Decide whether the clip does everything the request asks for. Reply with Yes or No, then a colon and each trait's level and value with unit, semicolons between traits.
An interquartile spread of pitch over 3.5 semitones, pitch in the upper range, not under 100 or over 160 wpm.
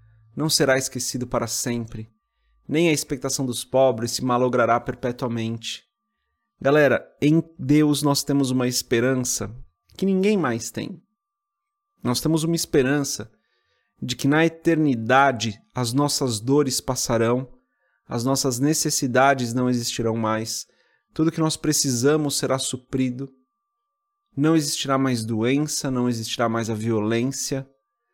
No: average, 4.0 semitones; low, 130 Hz; average, 125 wpm